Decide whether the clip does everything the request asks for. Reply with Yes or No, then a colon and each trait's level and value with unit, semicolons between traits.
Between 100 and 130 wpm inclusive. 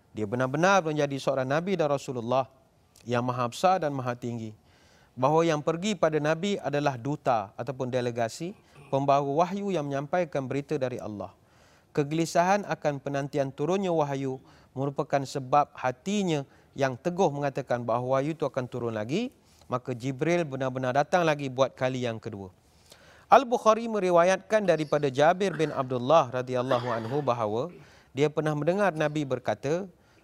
No: average, 140 wpm